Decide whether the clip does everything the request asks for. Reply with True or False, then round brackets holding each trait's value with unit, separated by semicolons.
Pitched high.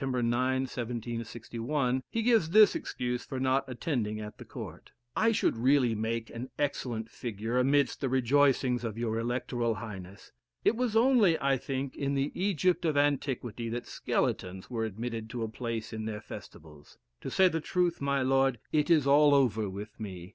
False (125 Hz)